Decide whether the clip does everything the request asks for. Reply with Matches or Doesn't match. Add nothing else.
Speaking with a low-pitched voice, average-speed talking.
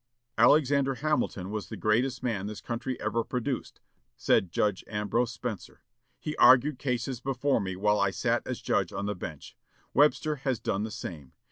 Matches